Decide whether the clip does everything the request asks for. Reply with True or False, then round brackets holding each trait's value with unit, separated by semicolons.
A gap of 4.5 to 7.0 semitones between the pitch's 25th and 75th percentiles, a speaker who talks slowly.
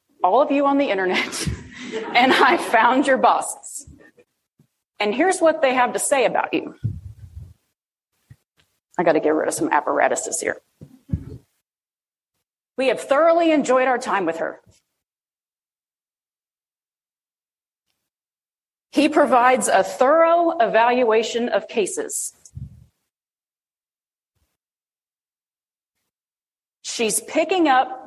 True (5.1 semitones; 100 wpm)